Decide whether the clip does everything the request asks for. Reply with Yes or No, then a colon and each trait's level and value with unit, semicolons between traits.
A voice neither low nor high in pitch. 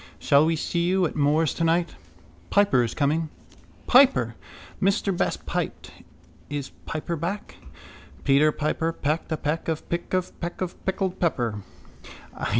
Yes: medium, 165 Hz